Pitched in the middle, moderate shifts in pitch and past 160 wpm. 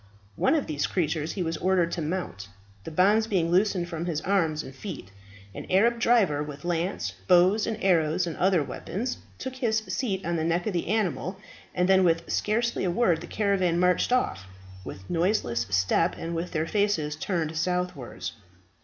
Yes: medium, 180 Hz; average, 3.6 semitones; average, 180 wpm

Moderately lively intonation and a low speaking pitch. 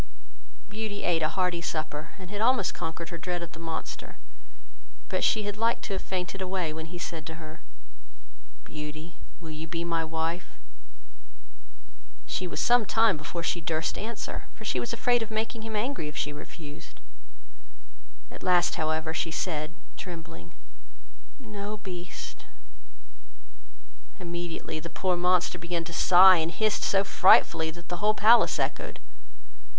No: average, 3.8 semitones; medium, 175 Hz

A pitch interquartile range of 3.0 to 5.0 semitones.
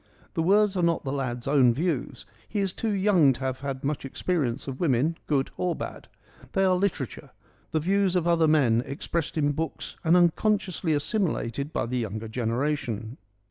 No: wide, 5.5 semitones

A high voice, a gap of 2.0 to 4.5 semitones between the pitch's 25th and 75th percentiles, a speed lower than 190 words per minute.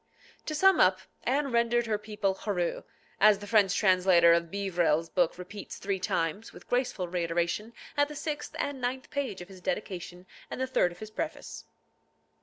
No: high, 200 Hz; average, 5.2 semitones; average, 175 wpm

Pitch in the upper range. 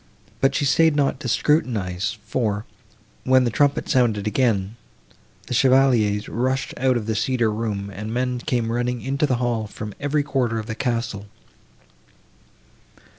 No: low, 120 Hz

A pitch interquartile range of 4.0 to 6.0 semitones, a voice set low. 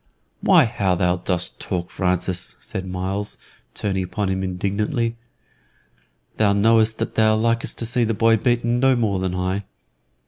No: average, 3.5 semitones; low, 100 Hz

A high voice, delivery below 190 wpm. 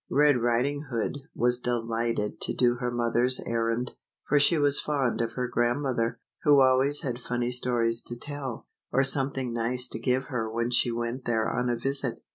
No: low, 125 Hz; average, 180 wpm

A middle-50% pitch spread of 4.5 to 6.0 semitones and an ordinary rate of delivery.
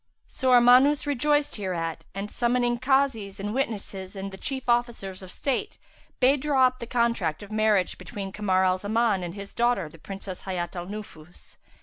Yes: average, 4.8 semitones; average, 175 wpm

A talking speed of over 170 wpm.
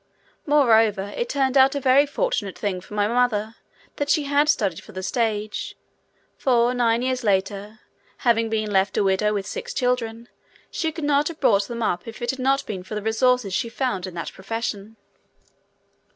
Yes: average, 185 wpm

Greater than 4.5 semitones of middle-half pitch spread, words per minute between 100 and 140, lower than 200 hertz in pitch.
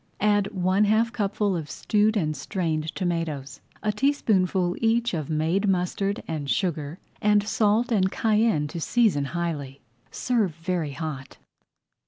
Yes: average, 5.2 semitones; slow, 135 wpm; medium, 185 Hz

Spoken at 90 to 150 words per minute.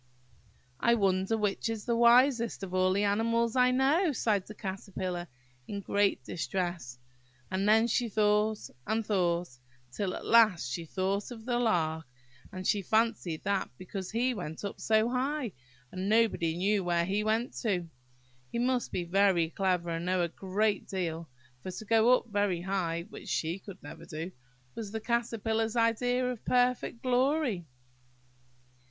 No: average, 160 wpm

